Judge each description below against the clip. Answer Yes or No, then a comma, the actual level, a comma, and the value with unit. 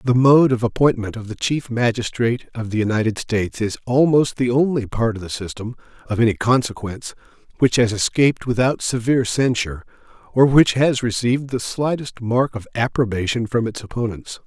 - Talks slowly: No, average, 170 wpm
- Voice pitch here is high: No, low, 120 Hz